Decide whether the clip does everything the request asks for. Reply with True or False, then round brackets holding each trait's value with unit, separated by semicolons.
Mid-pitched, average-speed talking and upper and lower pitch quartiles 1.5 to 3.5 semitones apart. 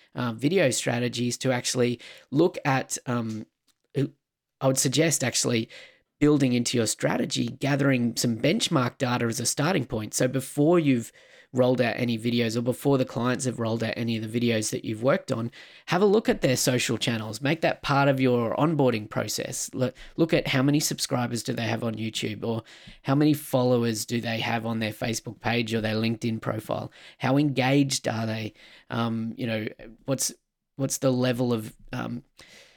False (125 Hz; 180 wpm; 2.9 semitones)